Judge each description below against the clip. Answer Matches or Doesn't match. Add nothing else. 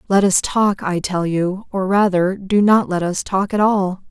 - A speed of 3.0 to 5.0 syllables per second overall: Matches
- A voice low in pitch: Doesn't match